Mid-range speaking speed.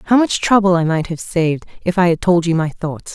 No: fast, 265 wpm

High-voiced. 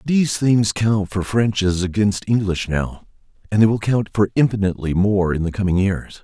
No: low, 100 Hz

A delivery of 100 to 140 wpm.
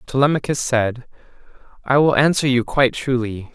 Yes: slow, 135 wpm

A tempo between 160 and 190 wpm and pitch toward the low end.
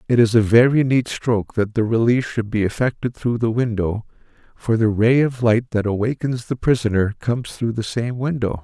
No: average, 200 wpm; low, 115 Hz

